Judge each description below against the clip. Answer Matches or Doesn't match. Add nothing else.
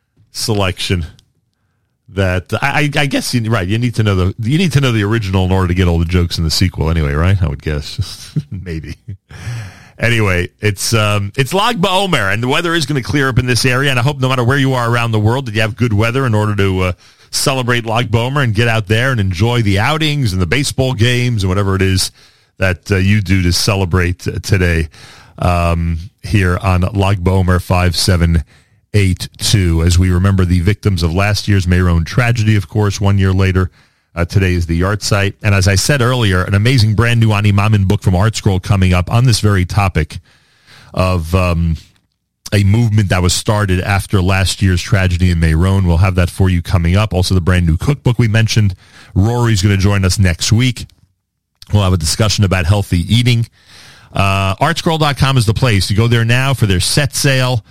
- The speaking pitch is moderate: Doesn't match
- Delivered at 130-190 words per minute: Doesn't match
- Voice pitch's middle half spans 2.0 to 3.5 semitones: Doesn't match